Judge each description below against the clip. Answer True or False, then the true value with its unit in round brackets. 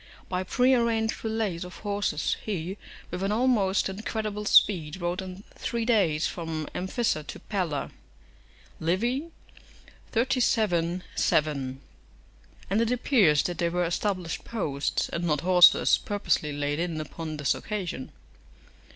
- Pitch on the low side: False (185 Hz)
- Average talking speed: False (125 wpm)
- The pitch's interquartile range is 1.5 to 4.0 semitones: False (5.0 semitones)